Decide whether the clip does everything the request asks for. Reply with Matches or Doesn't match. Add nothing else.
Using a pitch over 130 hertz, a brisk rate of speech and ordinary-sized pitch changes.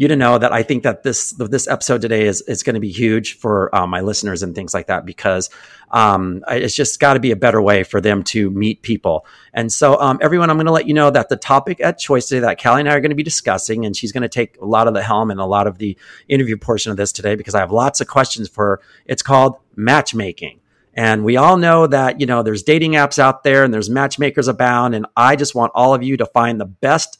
Doesn't match